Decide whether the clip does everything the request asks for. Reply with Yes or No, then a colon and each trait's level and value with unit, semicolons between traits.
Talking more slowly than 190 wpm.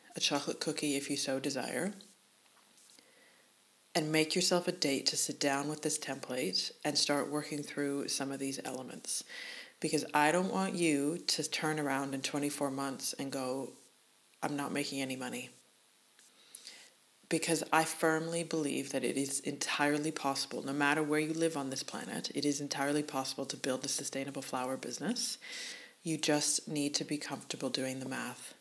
Yes: average, 170 wpm